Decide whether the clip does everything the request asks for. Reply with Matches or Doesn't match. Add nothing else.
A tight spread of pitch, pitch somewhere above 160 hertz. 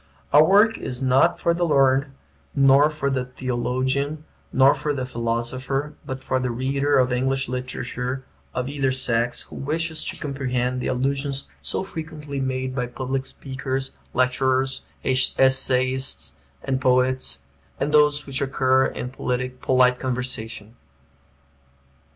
Doesn't match